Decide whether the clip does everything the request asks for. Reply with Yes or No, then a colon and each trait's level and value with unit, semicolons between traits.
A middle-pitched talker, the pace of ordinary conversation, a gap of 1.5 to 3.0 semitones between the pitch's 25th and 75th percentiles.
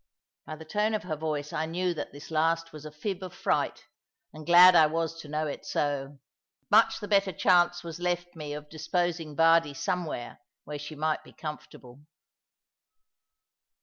Yes: medium, 160 Hz; average, 175 wpm; narrow, 2.6 semitones